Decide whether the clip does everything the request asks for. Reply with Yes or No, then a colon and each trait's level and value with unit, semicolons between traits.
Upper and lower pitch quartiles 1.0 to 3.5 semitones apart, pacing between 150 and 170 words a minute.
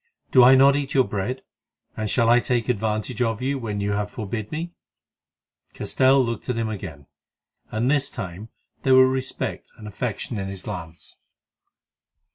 No: average, 4.0 semitones; average, 165 wpm